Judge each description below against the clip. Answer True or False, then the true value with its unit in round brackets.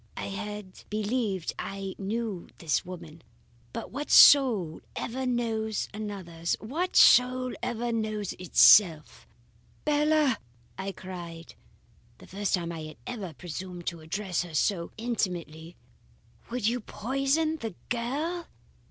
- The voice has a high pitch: True (210 Hz)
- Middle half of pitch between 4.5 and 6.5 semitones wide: True (5.6 semitones)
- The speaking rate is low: True (120 wpm)